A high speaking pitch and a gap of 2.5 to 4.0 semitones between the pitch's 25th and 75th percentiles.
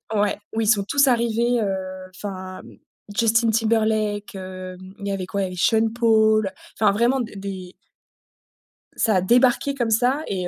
Yes: high, 215 Hz; average, 3.3 semitones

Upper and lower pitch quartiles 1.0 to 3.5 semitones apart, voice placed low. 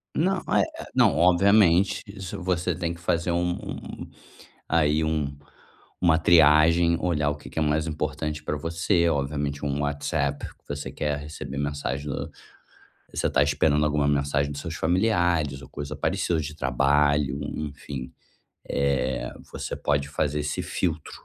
Yes: average, 2.8 semitones; very low, 75 Hz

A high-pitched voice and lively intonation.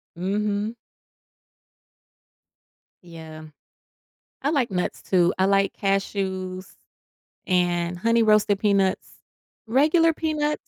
No: high, 195 Hz; average, 3.9 semitones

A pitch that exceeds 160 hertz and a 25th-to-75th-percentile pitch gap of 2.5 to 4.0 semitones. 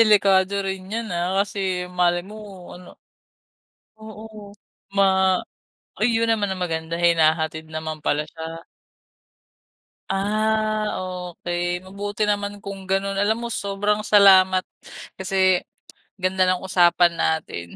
Yes: high, 190 Hz; average, 2.8 semitones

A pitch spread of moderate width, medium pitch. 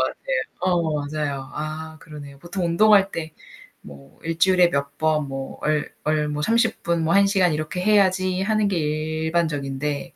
Yes: average, 3.8 semitones; medium, 160 Hz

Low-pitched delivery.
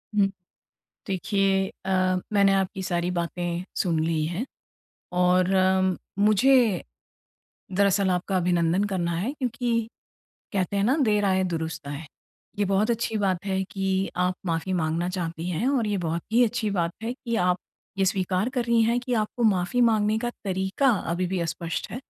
No: high, 190 Hz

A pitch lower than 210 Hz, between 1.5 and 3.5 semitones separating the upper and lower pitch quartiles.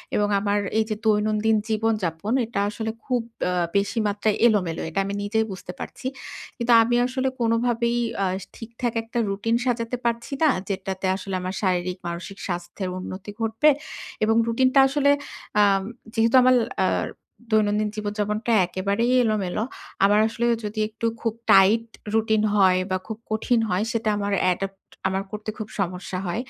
No: high, 215 Hz; average, 2.8 semitones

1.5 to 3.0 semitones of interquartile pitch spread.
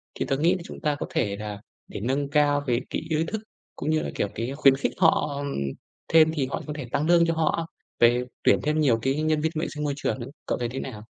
No: average, 3.8 semitones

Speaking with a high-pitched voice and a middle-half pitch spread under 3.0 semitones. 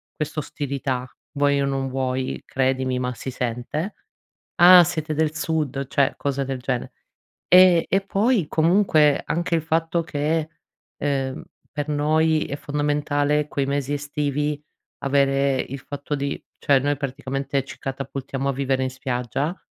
No: medium, 145 Hz; narrow, 2.4 semitones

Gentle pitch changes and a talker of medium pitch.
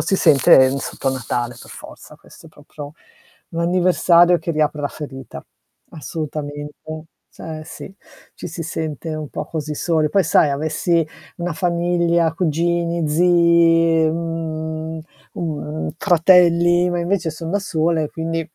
Yes: narrow, 1.9 semitones; medium, 165 Hz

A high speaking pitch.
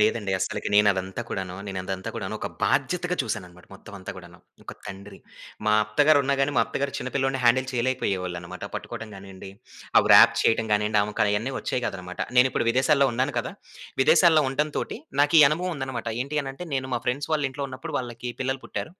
No: low, 125 Hz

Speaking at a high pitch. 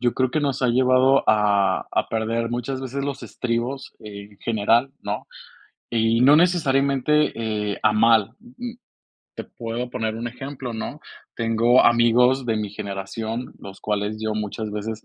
No: low, 115 Hz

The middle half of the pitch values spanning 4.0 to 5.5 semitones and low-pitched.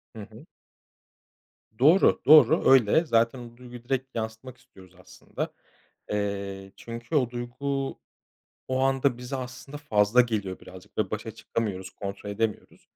Yes: average, 4.3 semitones; low, 120 Hz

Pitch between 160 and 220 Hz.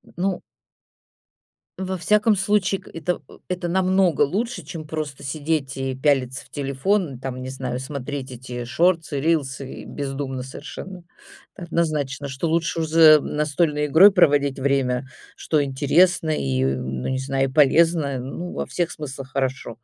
No: medium, 145 Hz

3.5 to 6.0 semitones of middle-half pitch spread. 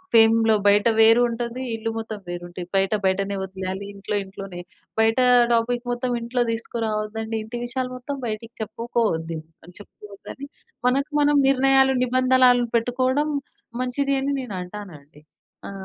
Yes: average, 3.9 semitones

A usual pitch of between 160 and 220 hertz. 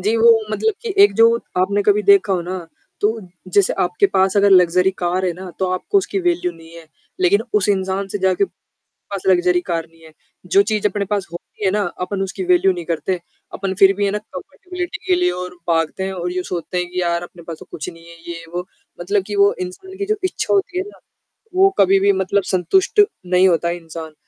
Yes: high, 190 Hz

